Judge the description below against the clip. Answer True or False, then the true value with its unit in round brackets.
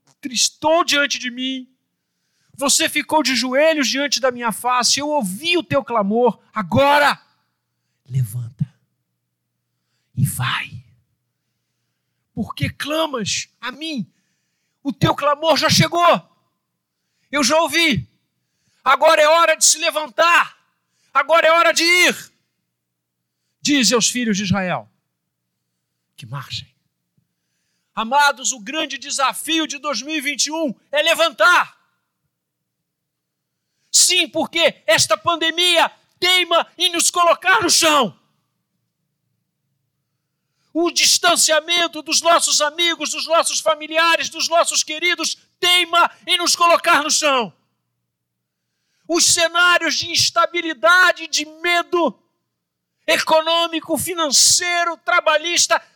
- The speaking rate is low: True (100 wpm)